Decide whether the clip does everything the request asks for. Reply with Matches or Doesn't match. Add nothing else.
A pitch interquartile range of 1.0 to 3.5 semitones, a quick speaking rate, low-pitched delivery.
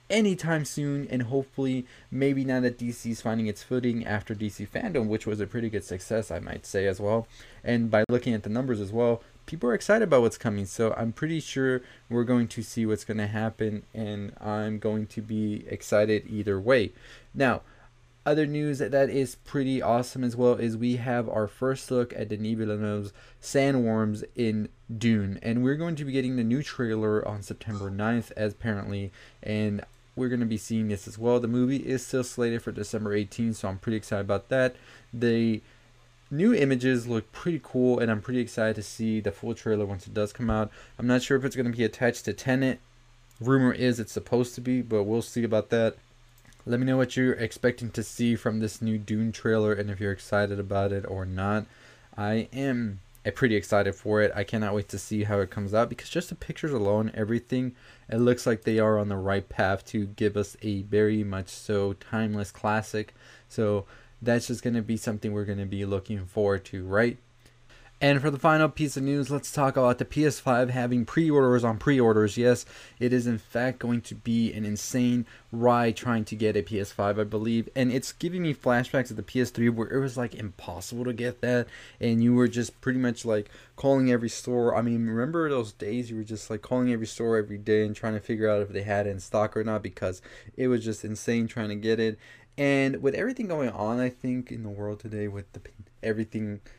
Matches